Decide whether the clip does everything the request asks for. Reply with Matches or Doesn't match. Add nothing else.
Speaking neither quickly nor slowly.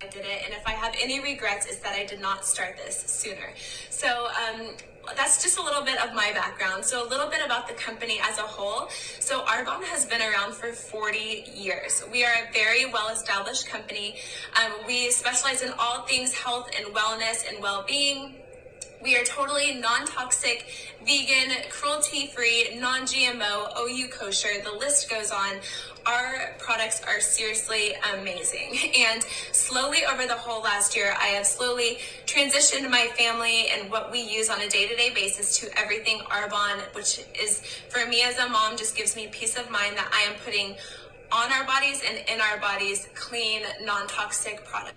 Matches